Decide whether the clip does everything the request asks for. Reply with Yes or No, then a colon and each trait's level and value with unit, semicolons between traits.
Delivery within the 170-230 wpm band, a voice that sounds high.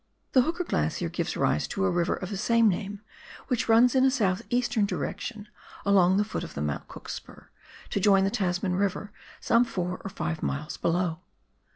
Yes: average, 195 wpm; high, 200 Hz